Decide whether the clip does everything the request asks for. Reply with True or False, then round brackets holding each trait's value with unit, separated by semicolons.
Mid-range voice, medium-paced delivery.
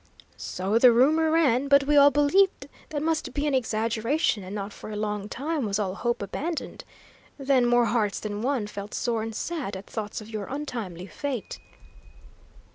False (240 Hz; 180 wpm)